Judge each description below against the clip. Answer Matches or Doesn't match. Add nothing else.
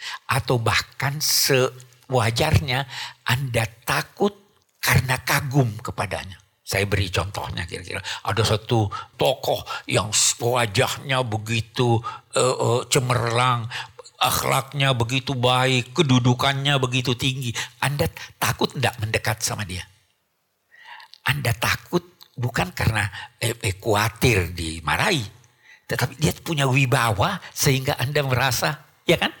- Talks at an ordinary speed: Matches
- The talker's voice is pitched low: Matches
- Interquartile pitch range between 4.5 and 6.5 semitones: Doesn't match